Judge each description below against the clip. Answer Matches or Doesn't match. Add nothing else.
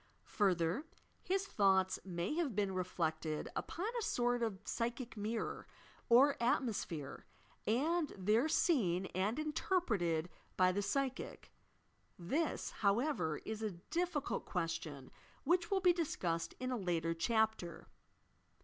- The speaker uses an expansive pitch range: Matches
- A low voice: Doesn't match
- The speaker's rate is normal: Doesn't match